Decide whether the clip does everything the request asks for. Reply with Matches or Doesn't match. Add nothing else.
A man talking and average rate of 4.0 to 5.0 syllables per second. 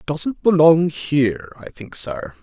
Matches